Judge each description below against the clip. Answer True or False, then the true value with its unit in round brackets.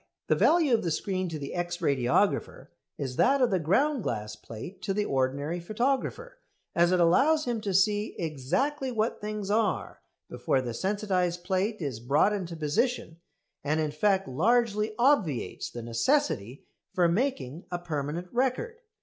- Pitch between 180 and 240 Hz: True (185 Hz)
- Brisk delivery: False (160 wpm)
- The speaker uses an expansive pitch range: True (7.0 semitones)